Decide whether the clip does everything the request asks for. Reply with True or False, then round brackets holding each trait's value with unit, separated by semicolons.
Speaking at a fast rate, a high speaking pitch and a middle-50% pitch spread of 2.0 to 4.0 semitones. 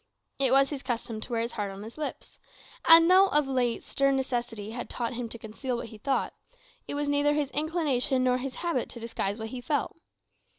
True (215 wpm; 255 Hz; 3.7 semitones)